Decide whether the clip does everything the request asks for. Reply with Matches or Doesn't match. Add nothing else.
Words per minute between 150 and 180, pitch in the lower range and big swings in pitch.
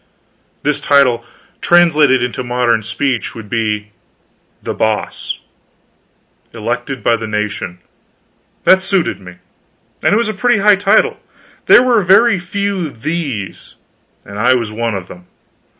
Doesn't match